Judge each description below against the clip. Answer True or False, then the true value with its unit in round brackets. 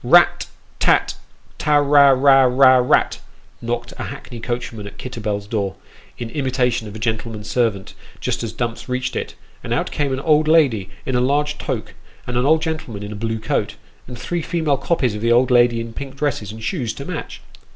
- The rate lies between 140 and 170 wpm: False (205 wpm)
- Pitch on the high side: False (125 Hz)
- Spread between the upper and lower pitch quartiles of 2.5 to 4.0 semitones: True (3.6 semitones)